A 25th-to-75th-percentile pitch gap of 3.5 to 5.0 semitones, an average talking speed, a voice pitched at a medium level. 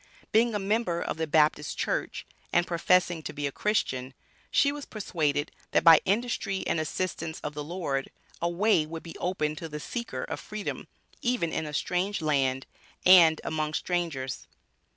Yes: average, 4.2 semitones; average, 170 wpm; medium, 165 Hz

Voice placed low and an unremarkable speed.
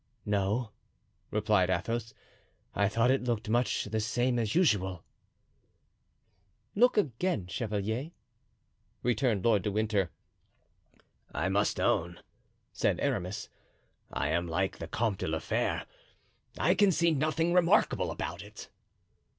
No: low, 110 Hz; slow, 115 wpm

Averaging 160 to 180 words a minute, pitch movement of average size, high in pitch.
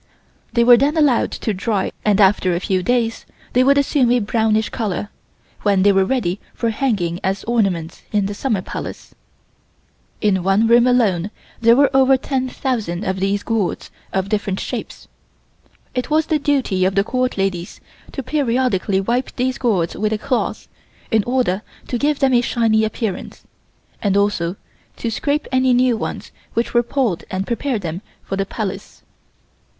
Yes: average, 165 wpm; average, 4.6 semitones; high, 220 Hz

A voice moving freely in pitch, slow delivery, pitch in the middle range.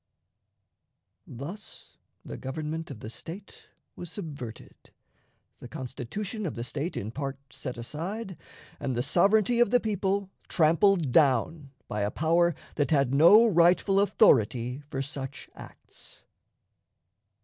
Yes: wide, 6.7 semitones; slow, 125 wpm; medium, 155 Hz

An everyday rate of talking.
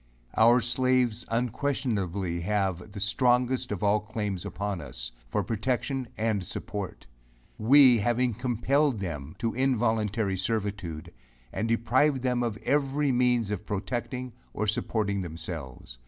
No: slow, 125 wpm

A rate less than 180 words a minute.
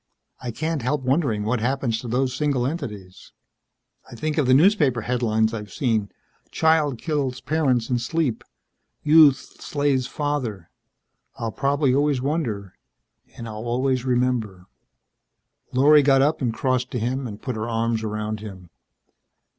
Yes: average, 145 wpm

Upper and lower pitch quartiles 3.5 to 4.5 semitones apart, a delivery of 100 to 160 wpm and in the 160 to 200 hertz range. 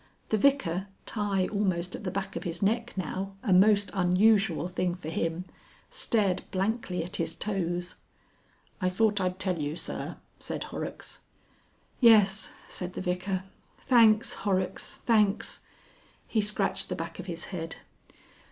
No: average, 2.7 semitones; average, 145 wpm; high, 190 Hz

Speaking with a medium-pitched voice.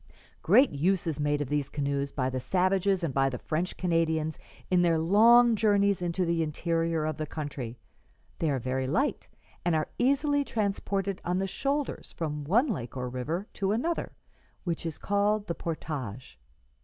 Yes: medium, 165 Hz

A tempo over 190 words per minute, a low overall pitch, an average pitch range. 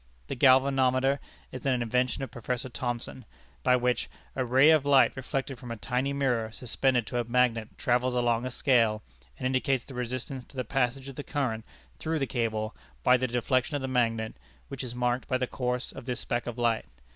No: average, 200 wpm; low, 125 Hz; narrow, 1.8 semitones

